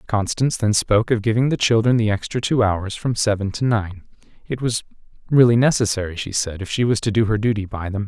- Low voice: Yes, low, 110 Hz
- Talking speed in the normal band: No, fast, 225 wpm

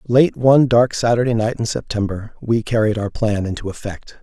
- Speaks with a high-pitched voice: No, low, 110 Hz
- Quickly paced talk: No, average, 185 wpm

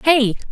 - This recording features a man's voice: No, female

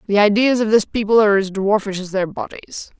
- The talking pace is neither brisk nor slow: No, fast, 220 wpm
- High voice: Yes, high, 205 Hz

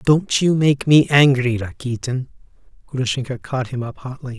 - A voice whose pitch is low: Yes, low, 130 Hz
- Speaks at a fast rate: No, average, 150 wpm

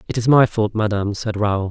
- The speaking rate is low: No, fast, 245 wpm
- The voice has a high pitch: No, low, 110 Hz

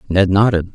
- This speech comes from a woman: No, male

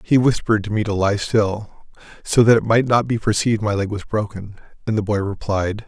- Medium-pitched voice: No, low, 105 Hz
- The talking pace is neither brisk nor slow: No, fast, 225 wpm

